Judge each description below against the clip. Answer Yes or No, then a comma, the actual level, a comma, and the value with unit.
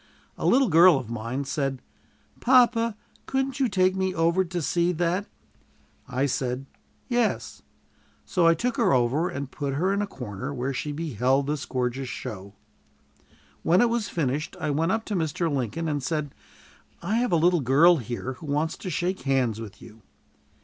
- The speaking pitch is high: No, medium, 155 Hz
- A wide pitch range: Yes, wide, 5.8 semitones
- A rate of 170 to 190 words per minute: Yes, average, 175 wpm